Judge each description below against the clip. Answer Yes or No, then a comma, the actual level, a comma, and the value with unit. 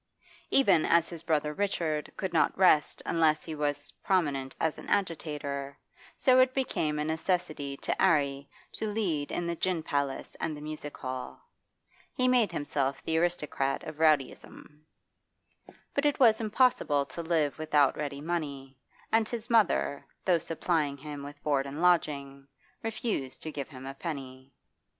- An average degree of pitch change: Yes, average, 3.8 semitones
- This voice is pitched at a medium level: Yes, medium, 155 Hz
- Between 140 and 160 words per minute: Yes, average, 155 wpm